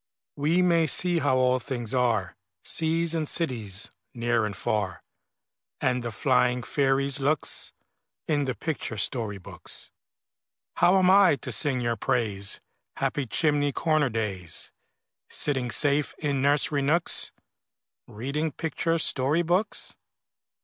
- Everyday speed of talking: No, slow, 125 wpm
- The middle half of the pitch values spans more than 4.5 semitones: Yes, average, 5.0 semitones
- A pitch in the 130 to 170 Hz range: Yes, low, 135 Hz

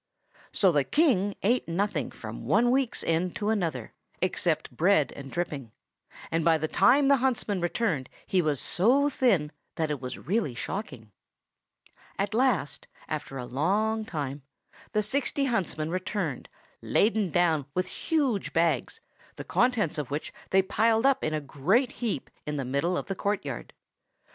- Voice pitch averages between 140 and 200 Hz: Yes, medium, 185 Hz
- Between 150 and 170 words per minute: Yes, average, 155 wpm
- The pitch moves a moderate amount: No, wide, 6.5 semitones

